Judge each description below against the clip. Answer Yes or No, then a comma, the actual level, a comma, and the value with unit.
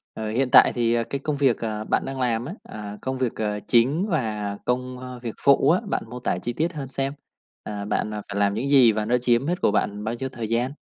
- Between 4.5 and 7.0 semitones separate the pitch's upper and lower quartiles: No, average, 3.7 semitones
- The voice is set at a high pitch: No, low, 120 Hz